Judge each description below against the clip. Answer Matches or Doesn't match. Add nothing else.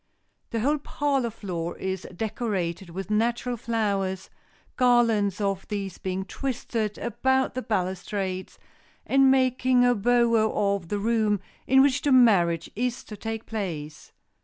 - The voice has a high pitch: Matches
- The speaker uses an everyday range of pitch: Matches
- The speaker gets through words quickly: Doesn't match